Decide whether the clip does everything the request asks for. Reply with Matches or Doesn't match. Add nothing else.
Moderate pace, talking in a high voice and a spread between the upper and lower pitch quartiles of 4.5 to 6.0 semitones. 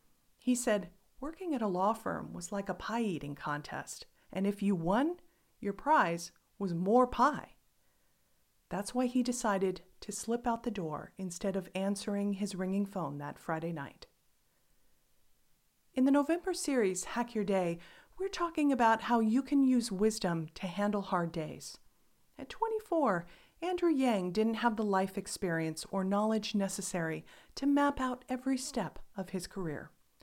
Matches